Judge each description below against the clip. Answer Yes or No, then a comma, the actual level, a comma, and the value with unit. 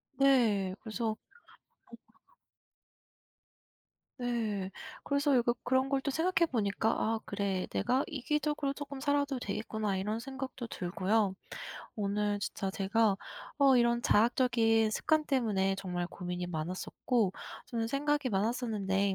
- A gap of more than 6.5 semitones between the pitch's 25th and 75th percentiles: No, average, 5.1 semitones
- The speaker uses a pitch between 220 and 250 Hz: Yes, high, 225 Hz